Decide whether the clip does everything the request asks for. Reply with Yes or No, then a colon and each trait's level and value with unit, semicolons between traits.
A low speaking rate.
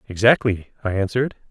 Yes: slow, 120 wpm